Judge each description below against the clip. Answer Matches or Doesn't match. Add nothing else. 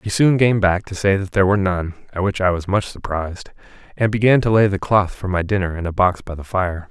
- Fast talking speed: Matches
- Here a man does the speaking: Matches